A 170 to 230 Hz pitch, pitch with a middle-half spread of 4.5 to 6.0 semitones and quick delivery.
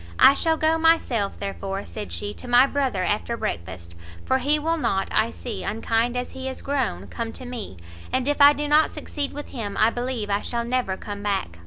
No: high, 240 Hz; wide, 5.6 semitones; fast, 210 wpm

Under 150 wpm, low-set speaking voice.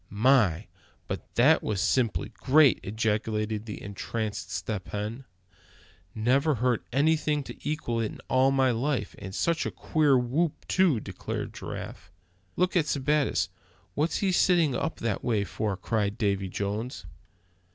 Yes: average, 140 wpm; low, 120 Hz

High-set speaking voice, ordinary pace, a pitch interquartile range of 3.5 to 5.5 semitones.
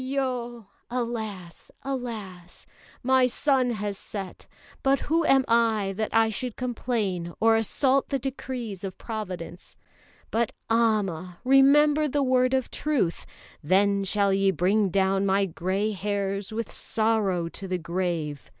No: high, 215 Hz; slow, 130 wpm; average, 4.7 semitones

